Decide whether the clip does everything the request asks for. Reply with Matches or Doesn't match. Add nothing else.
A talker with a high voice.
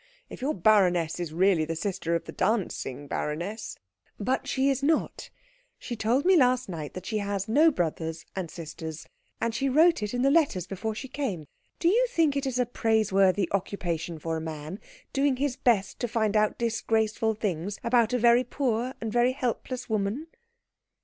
Matches